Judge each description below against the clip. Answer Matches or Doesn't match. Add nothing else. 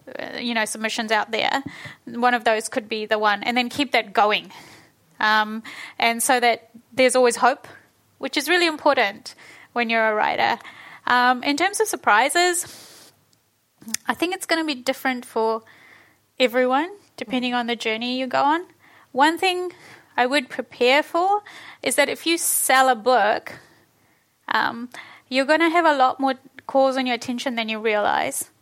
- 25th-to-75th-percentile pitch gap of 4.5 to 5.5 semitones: Doesn't match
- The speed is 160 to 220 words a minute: Matches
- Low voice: Doesn't match